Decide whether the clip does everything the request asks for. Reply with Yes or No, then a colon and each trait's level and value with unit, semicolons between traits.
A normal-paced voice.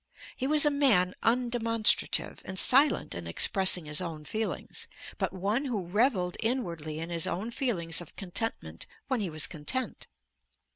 Yes: average, 150 wpm